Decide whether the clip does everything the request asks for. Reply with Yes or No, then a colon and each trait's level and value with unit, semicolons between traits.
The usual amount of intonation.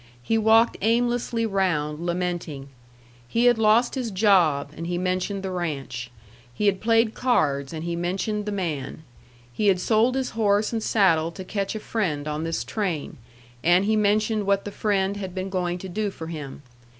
Yes: average, 4.4 semitones